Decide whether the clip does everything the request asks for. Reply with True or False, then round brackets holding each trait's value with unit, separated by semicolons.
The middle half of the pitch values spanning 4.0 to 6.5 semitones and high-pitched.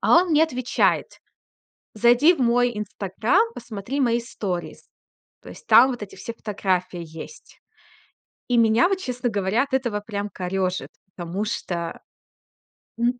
True (4.4 semitones; 230 Hz)